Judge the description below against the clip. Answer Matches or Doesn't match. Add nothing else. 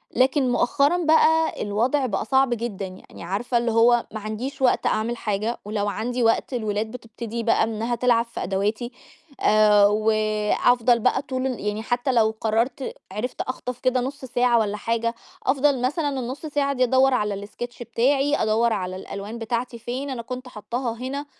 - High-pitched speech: Matches